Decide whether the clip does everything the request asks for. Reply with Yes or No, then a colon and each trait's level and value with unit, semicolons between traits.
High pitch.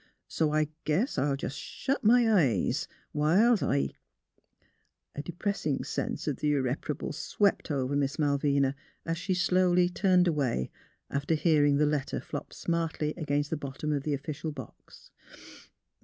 No: medium, 150 Hz